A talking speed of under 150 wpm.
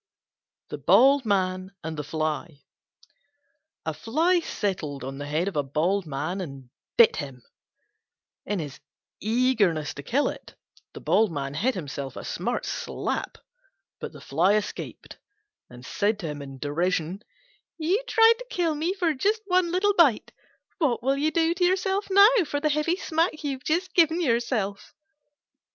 No: average, 155 wpm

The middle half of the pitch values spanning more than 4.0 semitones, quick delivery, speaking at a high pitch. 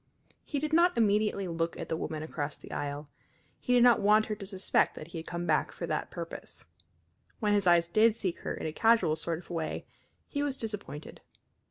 Yes: wide, 5.5 semitones; fast, 210 wpm; high, 195 Hz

